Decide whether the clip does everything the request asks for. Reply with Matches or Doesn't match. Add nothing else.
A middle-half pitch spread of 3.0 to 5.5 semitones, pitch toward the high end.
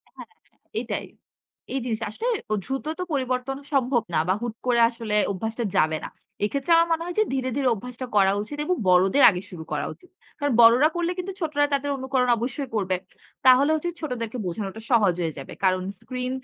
Matches